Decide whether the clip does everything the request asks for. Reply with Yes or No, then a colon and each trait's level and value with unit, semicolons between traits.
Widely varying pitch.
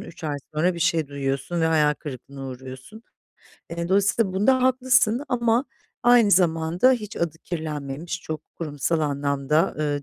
Yes: wide, 6.0 semitones